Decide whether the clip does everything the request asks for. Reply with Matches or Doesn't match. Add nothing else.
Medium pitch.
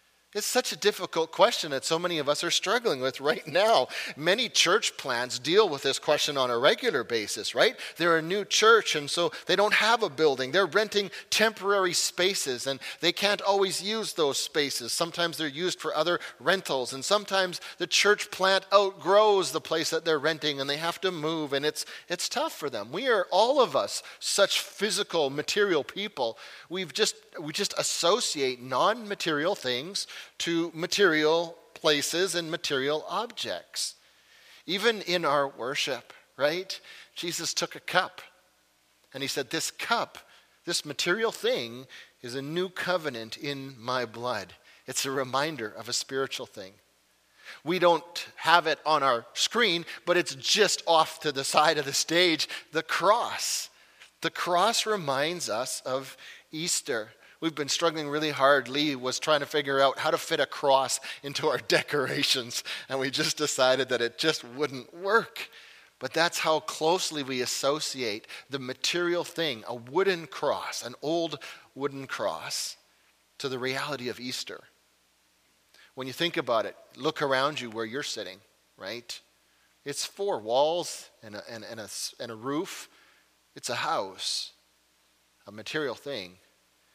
Matches